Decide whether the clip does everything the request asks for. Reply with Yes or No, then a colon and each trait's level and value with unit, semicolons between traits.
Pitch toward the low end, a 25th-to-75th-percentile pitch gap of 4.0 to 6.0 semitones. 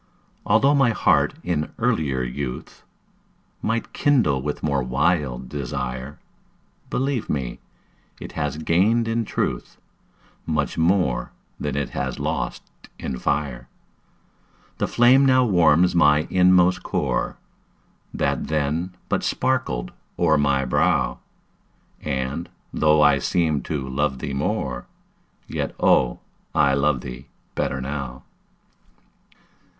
Yes: very low, 75 Hz; average, 5.1 semitones